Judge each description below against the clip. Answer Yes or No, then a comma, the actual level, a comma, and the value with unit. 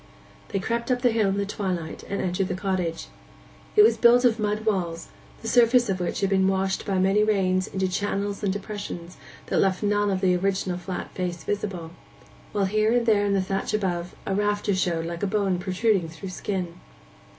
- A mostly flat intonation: Yes, narrow, 2.2 semitones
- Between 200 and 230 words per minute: Yes, fast, 205 wpm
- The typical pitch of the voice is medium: No, high, 195 Hz